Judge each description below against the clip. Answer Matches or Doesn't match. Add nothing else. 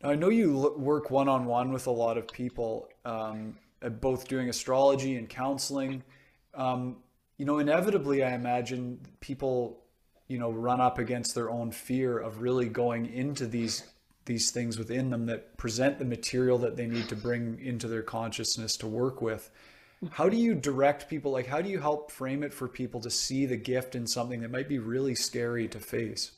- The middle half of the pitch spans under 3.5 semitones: Matches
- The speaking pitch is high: Doesn't match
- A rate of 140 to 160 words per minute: Doesn't match